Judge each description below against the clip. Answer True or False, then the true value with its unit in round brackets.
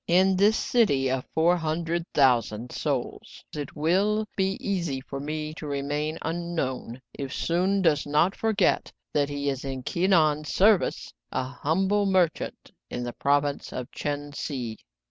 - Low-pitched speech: False (155 Hz)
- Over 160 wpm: False (155 wpm)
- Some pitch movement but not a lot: True (4.5 semitones)